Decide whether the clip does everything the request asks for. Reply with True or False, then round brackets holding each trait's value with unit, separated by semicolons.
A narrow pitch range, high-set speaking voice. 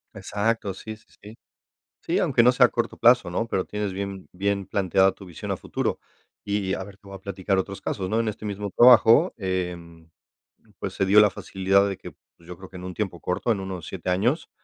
False (2.2 semitones; 100 Hz)